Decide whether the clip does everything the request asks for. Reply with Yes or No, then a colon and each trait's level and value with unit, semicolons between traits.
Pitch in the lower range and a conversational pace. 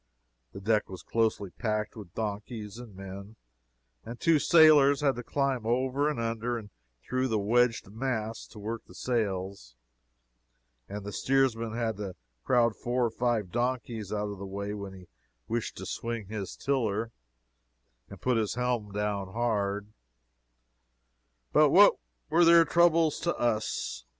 Yes: low, 115 Hz; average, 150 wpm